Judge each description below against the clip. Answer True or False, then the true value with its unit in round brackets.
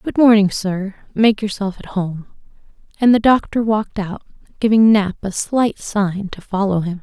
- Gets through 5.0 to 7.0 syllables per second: False (4.6 syllables/s)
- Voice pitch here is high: True (205 Hz)